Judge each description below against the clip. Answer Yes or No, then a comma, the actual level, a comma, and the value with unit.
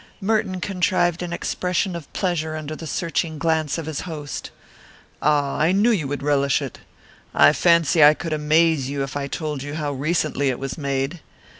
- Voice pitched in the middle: Yes, medium, 155 Hz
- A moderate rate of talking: Yes, average, 180 wpm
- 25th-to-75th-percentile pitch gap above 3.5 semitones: No, average, 3.1 semitones